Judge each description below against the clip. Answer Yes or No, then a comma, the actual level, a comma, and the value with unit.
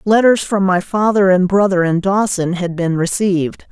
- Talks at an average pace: Yes, average, 180 wpm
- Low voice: No, high, 190 Hz